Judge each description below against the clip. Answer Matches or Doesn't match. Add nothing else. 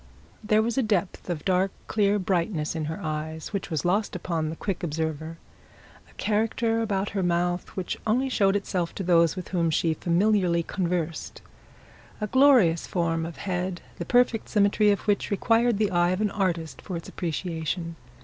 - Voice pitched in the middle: Matches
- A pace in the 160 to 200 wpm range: Matches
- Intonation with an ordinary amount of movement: Matches